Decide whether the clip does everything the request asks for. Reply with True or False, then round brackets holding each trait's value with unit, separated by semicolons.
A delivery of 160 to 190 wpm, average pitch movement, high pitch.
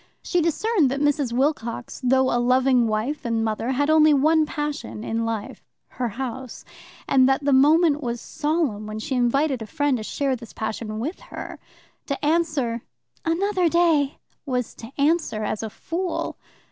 True (165 wpm; 4.6 semitones; 270 Hz)